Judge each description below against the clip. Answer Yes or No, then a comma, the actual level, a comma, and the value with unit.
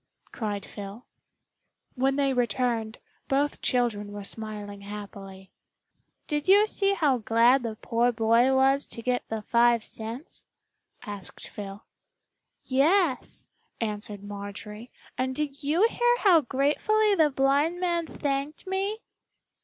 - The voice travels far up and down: Yes, wide, 5.7 semitones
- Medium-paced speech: No, slow, 120 wpm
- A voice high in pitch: Yes, very high, 250 Hz